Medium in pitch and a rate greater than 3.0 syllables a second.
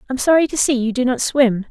No: very high, 255 Hz; 6.0 syllables/s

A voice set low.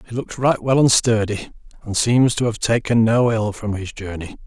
Yes: low, 115 Hz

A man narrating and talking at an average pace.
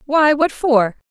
No: female; average, 165 wpm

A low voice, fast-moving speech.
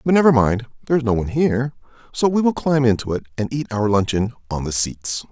Yes: low, 120 Hz; fast, 225 wpm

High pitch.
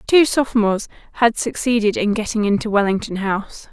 Yes: high, 220 Hz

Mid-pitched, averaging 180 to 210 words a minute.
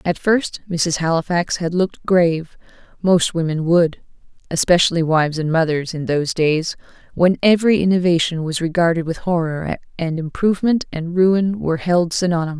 No: medium, 170 Hz; average, 145 wpm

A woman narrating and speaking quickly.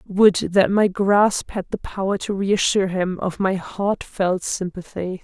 No: female; average, 160 wpm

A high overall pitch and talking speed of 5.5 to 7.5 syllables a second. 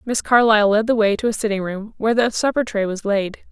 Yes: high, 215 Hz; 6.1 syllables/s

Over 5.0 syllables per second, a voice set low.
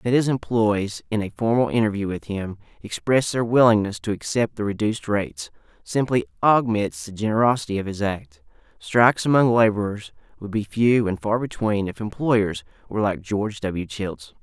Yes: 5.2 syllables/s; low, 110 Hz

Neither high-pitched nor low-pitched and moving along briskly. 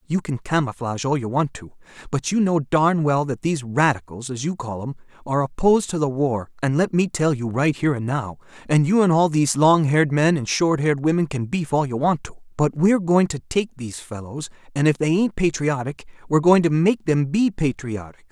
Yes: medium, 145 Hz; fast, 230 wpm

